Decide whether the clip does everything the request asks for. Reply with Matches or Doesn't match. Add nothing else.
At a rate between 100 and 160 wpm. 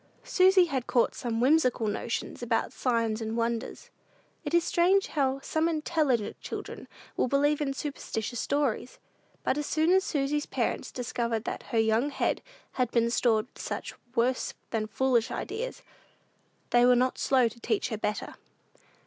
Matches